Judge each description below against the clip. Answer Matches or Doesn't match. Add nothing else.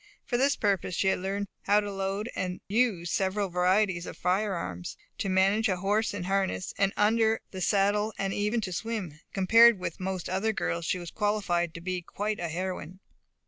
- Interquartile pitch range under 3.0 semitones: Matches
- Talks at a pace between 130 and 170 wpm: Doesn't match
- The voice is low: Doesn't match